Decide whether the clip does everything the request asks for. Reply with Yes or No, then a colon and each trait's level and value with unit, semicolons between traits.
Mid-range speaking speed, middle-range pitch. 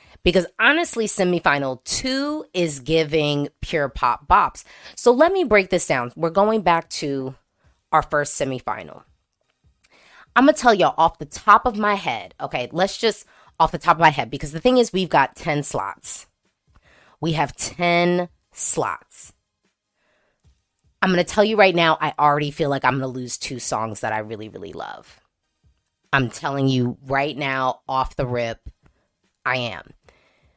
Yes: average, 170 wpm; medium, 155 Hz